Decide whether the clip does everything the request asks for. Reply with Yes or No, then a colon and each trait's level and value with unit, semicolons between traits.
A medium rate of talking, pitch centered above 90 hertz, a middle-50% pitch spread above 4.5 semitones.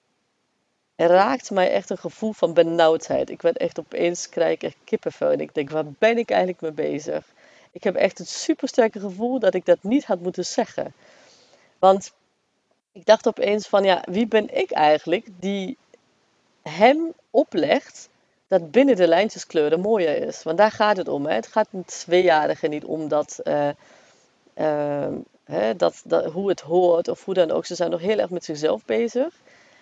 Yes: average, 180 wpm; high, 190 Hz; wide, 5.4 semitones